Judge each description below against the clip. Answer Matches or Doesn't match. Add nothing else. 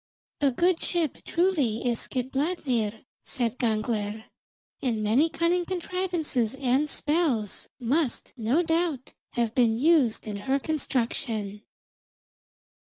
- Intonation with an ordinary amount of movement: Doesn't match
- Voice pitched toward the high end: Matches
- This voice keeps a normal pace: Doesn't match